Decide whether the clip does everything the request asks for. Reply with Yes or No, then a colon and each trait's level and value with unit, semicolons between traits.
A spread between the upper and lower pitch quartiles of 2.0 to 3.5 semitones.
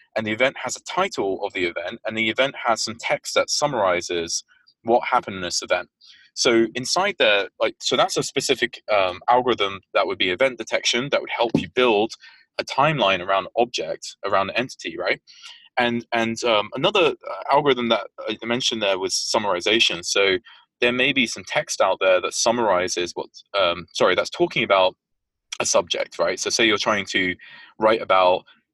No: average, 4.1 semitones